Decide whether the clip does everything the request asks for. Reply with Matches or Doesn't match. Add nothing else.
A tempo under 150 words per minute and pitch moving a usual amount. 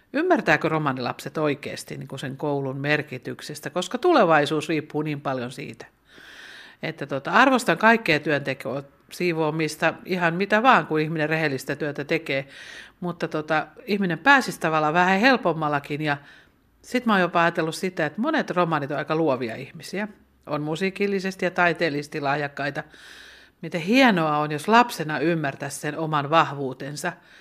Matches